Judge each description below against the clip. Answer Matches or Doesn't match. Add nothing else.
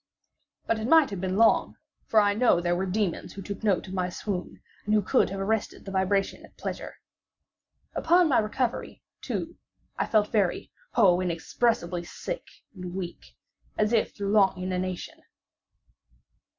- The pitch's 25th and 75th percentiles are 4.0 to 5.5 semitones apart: Doesn't match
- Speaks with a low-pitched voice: Doesn't match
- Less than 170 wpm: Matches